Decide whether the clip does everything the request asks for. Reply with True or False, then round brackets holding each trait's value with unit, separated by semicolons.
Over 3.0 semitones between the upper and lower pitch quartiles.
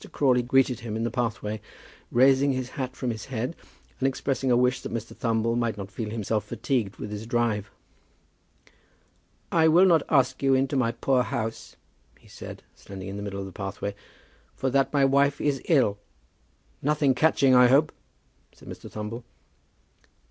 True (3.6 semitones)